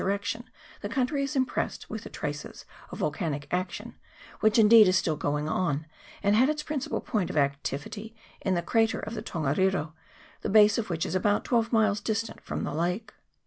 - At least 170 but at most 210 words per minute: Yes, average, 190 wpm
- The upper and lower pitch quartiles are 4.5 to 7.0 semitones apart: Yes, average, 5.1 semitones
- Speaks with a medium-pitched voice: No, high, 205 Hz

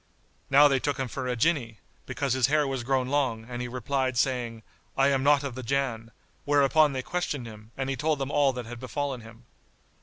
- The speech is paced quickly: Yes, fast, 215 wpm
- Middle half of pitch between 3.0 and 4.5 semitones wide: No, narrow, 2.6 semitones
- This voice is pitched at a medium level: No, low, 130 Hz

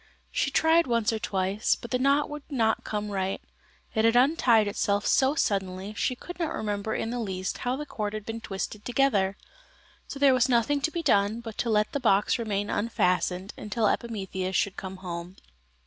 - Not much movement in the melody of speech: No, average, 4.1 semitones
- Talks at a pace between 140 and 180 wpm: No, average, 195 wpm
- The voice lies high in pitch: Yes, high, 220 Hz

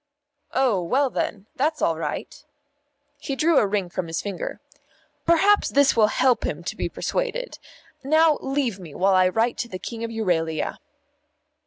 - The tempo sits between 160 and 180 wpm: Yes, average, 165 wpm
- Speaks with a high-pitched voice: Yes, high, 230 Hz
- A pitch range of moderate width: No, wide, 7.4 semitones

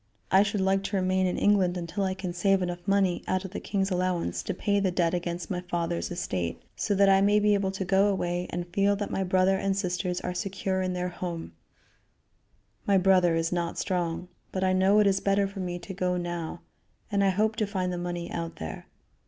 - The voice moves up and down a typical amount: No, narrow, 1.8 semitones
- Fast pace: Yes, fast, 225 wpm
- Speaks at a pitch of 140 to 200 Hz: Yes, medium, 185 Hz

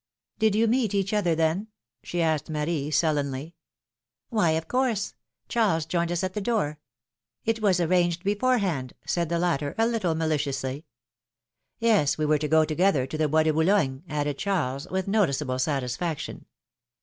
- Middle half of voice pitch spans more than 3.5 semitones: Yes, average, 4.9 semitones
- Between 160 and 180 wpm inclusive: Yes, average, 165 wpm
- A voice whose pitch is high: No, medium, 165 Hz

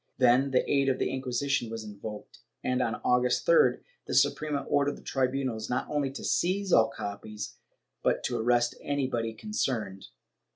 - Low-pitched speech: Yes, low, 125 Hz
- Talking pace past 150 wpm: Yes, average, 160 wpm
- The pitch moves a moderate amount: Yes, average, 3.7 semitones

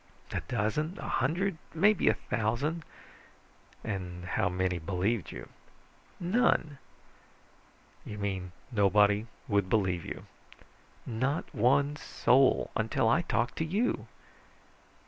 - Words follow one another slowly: Yes, slow, 105 wpm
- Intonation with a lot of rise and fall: Yes, wide, 7.5 semitones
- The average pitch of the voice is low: Yes, low, 115 Hz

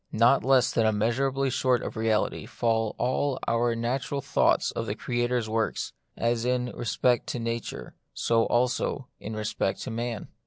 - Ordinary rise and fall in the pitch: No, narrow, 1.9 semitones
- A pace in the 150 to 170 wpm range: Yes, average, 160 wpm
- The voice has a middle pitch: No, low, 120 Hz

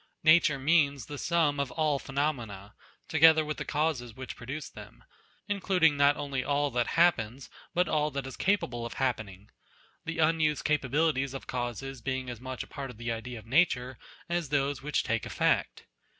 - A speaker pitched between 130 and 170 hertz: Yes, medium, 140 Hz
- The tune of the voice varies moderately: Yes, average, 3.9 semitones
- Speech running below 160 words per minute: No, average, 180 wpm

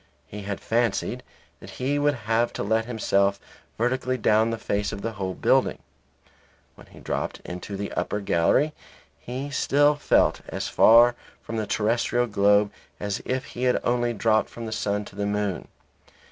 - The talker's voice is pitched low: Yes, low, 110 Hz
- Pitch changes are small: No, average, 3.1 semitones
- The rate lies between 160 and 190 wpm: Yes, average, 170 wpm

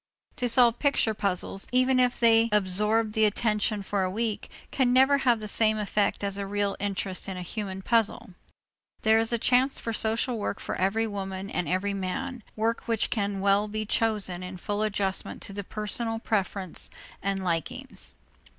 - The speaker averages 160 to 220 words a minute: Yes, average, 180 wpm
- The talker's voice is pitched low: No, high, 210 Hz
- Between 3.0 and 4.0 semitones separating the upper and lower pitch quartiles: No, narrow, 2.6 semitones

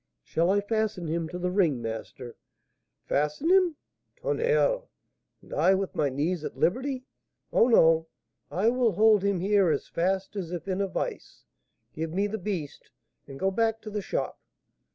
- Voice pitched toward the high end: Yes, high, 195 Hz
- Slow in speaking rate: No, average, 170 wpm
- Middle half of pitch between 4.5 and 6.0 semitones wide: Yes, average, 5.0 semitones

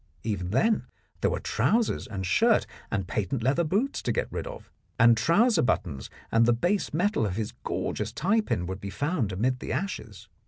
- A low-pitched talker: Yes, low, 120 Hz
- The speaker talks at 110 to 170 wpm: No, average, 190 wpm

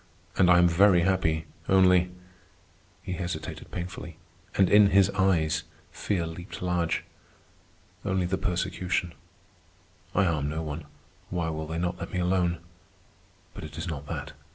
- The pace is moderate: Yes, average, 150 wpm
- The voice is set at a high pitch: No, very low, 90 Hz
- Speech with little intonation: Yes, narrow, 2.2 semitones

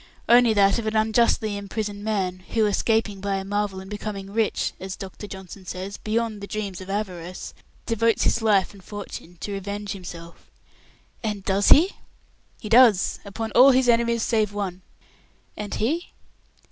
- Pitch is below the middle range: No, high, 205 Hz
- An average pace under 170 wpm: Yes, average, 160 wpm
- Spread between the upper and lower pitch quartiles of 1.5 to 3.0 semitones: Yes, narrow, 2.4 semitones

